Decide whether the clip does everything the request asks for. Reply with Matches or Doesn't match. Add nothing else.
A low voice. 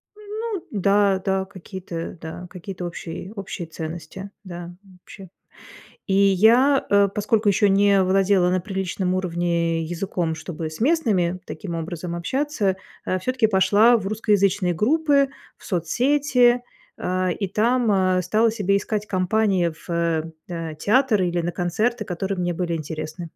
Doesn't match